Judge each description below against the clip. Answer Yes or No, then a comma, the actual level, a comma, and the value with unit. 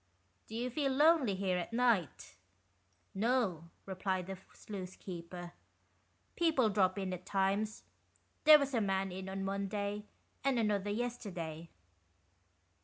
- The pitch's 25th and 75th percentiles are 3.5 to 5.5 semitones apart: Yes, average, 4.1 semitones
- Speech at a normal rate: No, slow, 130 wpm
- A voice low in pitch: No, high, 195 Hz